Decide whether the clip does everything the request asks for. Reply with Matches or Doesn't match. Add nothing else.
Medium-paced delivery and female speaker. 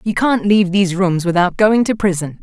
Doesn't match